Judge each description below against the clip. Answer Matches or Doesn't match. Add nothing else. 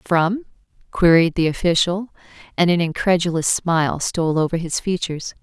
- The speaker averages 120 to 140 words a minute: Matches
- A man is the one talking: Doesn't match